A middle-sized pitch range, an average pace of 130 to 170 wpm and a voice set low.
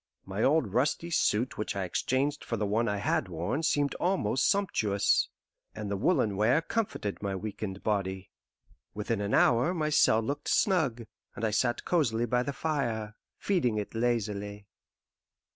No: wide, 5.8 semitones; average, 160 wpm; low, 115 Hz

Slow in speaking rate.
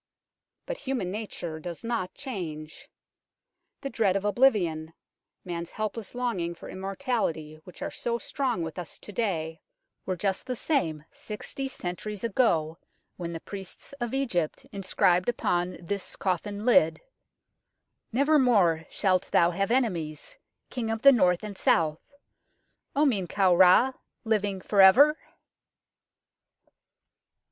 Yes: slow, 130 wpm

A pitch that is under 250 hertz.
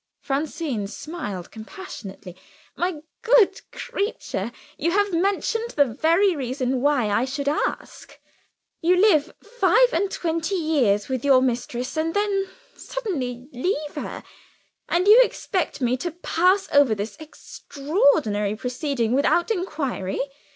No: very high, 300 Hz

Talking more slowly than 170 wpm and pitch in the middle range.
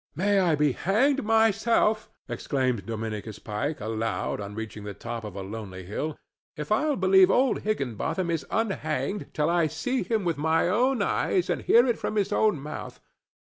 No: average, 175 wpm; medium, 165 Hz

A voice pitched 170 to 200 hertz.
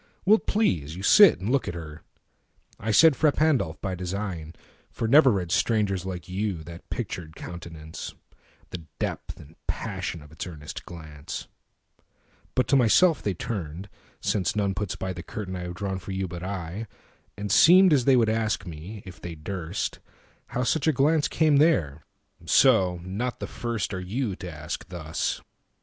No: very low, 95 Hz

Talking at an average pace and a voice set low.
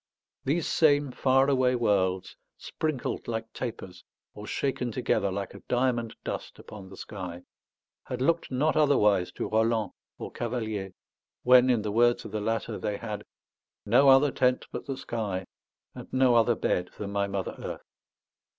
Yes: average, 160 wpm; low, 115 Hz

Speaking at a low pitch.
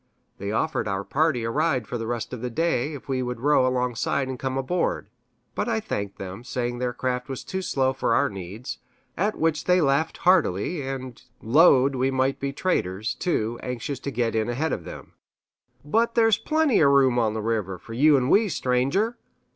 Yes: low, 130 Hz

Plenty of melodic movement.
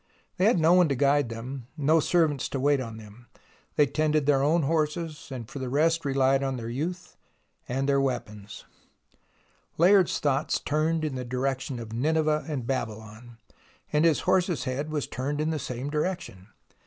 No: average, 3.6 semitones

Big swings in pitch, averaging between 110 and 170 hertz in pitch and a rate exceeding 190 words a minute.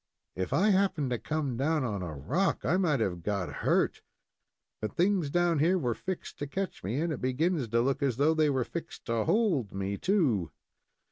Yes: wide, 7.1 semitones; medium, 140 Hz; average, 200 wpm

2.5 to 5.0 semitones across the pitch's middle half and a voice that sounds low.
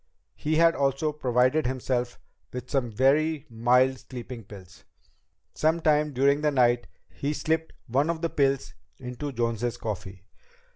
Yes: average, 3.7 semitones; low, 130 Hz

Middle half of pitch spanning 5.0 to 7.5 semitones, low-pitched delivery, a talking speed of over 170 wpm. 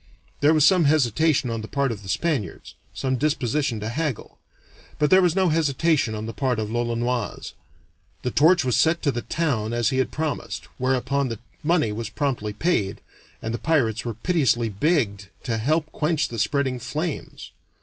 Yes: wide, 5.4 semitones; low, 130 Hz; average, 180 wpm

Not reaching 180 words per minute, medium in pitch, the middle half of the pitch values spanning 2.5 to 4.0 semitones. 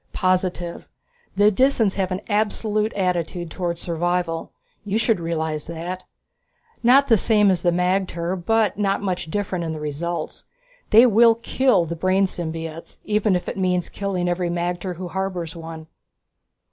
Yes: average, 150 wpm; medium, 180 Hz; average, 3.1 semitones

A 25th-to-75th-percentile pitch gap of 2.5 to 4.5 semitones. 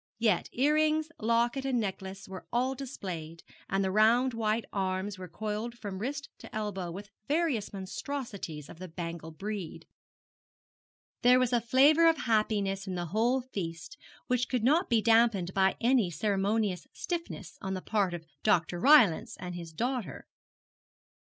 No: average, 5.0 semitones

